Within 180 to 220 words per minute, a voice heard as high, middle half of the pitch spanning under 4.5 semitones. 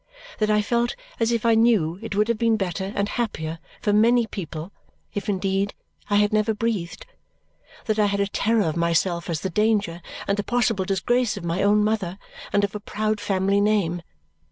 Yes: average, 195 wpm; high, 205 Hz; narrow, 2.5 semitones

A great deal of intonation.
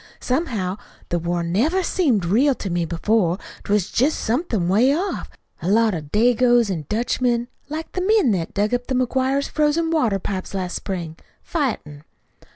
Yes: wide, 6.9 semitones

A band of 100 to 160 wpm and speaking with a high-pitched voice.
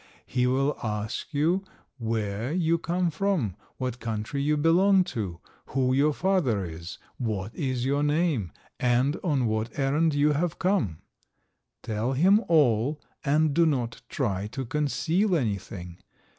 No: average, 140 wpm; low, 135 Hz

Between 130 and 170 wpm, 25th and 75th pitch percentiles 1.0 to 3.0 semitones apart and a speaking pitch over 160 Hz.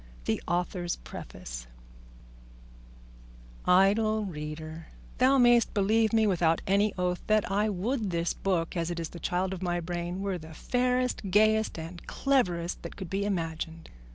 No: average, 150 wpm; average, 4.1 semitones; medium, 185 Hz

